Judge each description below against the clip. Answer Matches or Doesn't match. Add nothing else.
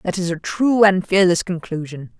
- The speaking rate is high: Doesn't match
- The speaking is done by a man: Doesn't match